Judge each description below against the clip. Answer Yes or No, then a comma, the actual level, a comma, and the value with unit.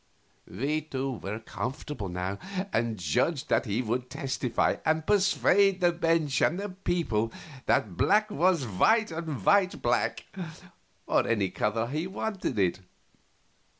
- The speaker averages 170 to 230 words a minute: No, average, 140 wpm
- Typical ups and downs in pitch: No, wide, 7.8 semitones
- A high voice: No, medium, 140 Hz